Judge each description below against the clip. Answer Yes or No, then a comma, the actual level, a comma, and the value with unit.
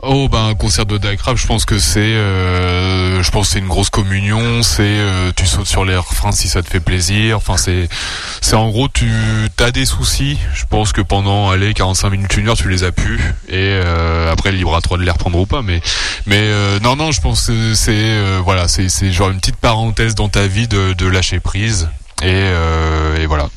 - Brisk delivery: Yes, fast, 230 wpm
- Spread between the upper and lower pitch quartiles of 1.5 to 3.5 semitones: Yes, average, 2.9 semitones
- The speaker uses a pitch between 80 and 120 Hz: Yes, low, 100 Hz